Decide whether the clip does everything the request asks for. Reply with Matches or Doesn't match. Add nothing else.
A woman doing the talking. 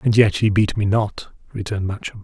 Doesn't match